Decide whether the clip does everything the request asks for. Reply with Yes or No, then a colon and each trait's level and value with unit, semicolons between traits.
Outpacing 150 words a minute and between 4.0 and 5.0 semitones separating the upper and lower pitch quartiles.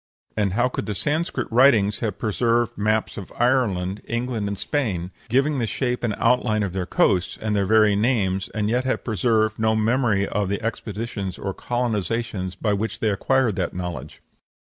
No: average, 175 wpm; average, 3.3 semitones